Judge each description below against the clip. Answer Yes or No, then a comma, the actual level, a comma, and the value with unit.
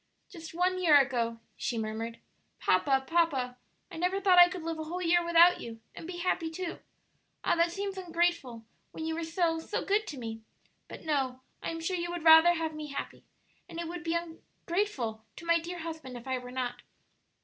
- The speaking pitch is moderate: No, very high, 330 Hz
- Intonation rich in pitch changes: No, average, 4.9 semitones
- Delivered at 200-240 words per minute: Yes, fast, 205 wpm